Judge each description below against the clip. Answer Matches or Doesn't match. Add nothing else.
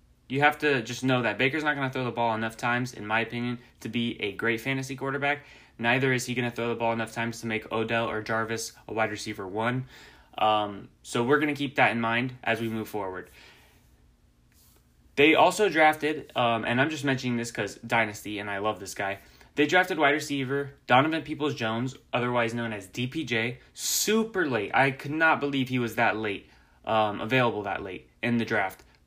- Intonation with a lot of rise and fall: Doesn't match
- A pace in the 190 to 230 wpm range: Matches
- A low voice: Matches